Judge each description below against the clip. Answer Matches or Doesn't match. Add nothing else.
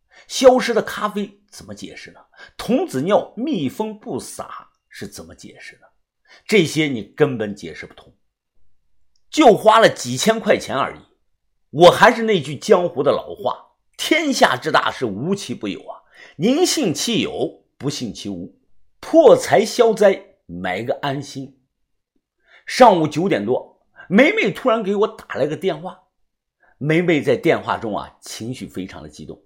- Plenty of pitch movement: Matches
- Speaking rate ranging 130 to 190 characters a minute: Doesn't match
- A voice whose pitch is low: Doesn't match